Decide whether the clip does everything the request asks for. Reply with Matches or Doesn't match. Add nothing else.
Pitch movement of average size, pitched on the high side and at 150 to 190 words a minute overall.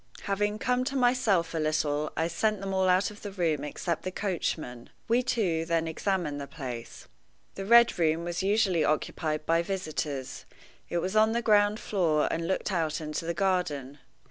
Doesn't match